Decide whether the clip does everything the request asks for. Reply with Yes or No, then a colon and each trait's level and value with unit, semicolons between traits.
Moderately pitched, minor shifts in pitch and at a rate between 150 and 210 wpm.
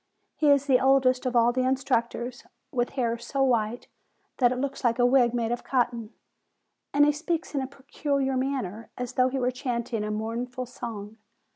No: very high, 250 Hz; narrow, 2.2 semitones; average, 185 wpm